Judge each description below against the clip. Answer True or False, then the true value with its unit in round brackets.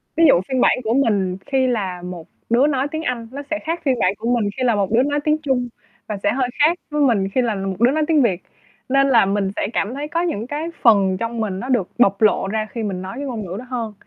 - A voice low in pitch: False (235 Hz)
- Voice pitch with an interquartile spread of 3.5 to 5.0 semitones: False (5.4 semitones)